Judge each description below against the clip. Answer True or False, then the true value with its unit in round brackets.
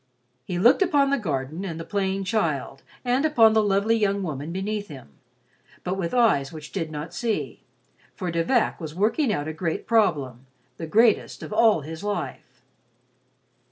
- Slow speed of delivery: False (170 wpm)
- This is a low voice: False (190 Hz)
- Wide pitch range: True (5.8 semitones)